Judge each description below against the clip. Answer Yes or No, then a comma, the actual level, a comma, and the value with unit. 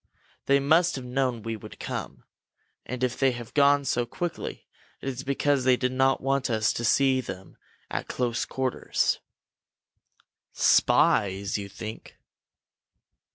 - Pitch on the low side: Yes, low, 130 Hz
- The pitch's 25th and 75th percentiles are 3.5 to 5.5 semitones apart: No, average, 2.7 semitones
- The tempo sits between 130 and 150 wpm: Yes, average, 140 wpm